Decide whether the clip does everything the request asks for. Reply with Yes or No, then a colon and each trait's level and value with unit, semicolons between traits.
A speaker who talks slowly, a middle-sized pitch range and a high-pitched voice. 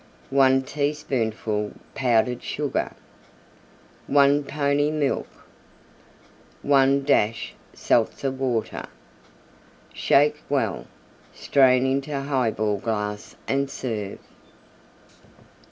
No: slow, 75 wpm; average, 3.8 semitones; low, 135 Hz